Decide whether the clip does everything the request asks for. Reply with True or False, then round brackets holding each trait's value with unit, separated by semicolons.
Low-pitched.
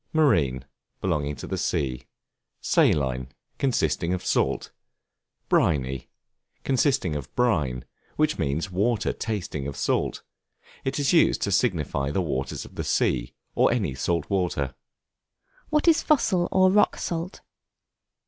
True (85 Hz)